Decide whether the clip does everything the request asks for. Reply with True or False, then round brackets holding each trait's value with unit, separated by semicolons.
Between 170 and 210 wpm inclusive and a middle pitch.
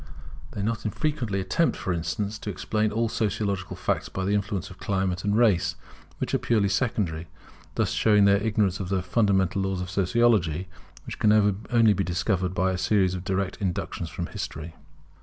False (175 wpm; 100 Hz)